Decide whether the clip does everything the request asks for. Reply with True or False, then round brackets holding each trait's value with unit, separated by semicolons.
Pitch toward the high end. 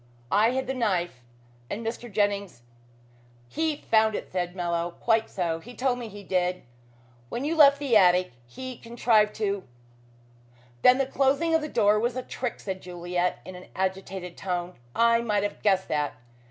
True (205 Hz)